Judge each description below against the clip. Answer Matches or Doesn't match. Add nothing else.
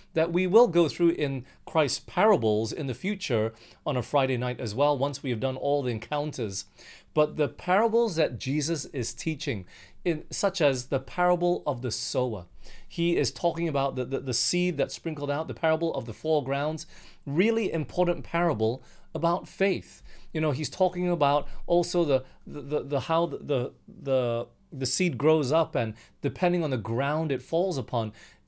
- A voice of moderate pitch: Matches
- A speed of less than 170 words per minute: Doesn't match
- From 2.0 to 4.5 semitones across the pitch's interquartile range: Doesn't match